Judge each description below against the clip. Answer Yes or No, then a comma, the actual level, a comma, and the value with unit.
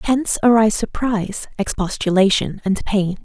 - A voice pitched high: Yes, high, 210 Hz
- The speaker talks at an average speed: No, slow, 110 wpm